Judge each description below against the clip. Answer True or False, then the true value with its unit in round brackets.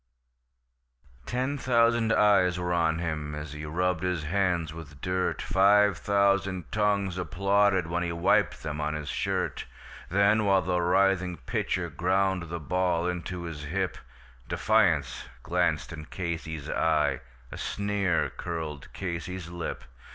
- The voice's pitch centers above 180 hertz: False (90 Hz)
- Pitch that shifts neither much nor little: True (3.1 semitones)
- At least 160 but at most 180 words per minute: False (135 wpm)